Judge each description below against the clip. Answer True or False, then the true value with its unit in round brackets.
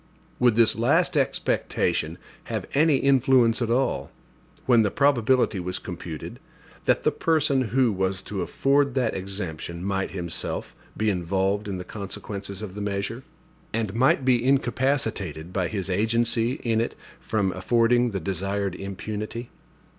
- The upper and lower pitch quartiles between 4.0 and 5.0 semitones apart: True (4.3 semitones)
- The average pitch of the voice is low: True (110 Hz)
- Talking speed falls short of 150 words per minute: True (140 wpm)